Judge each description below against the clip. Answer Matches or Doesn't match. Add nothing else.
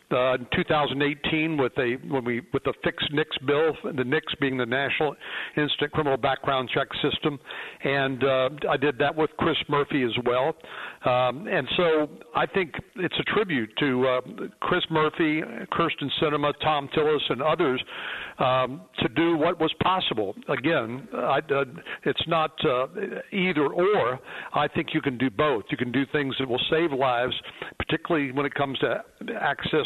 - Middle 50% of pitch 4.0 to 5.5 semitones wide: Doesn't match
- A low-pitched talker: Doesn't match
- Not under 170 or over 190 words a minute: Doesn't match